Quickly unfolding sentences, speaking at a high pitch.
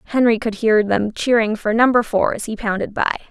Yes: fast, 220 wpm; high, 220 Hz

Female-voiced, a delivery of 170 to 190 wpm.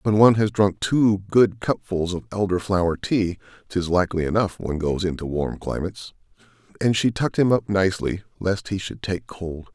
No: male; average, 185 wpm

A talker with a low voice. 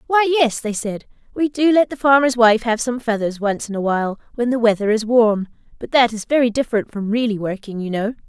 No: high, 230 Hz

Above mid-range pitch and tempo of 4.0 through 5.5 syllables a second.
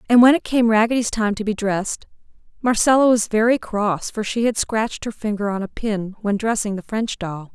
Yes: high, 215 Hz; 5.3 syllables/s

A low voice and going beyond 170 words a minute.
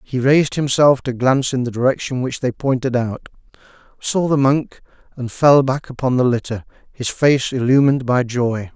Yes: low, 130 Hz; average, 180 wpm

